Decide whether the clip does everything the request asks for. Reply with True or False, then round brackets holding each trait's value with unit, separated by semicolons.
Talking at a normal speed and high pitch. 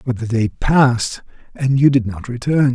False (195 wpm; 125 Hz)